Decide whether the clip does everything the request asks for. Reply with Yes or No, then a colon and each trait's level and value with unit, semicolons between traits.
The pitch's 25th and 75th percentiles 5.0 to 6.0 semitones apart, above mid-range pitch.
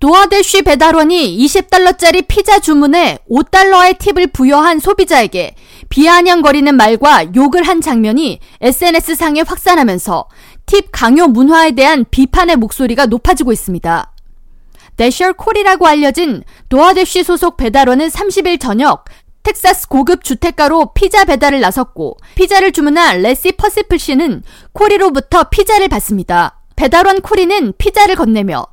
Yes: wide, 5.5 semitones; very high, 325 Hz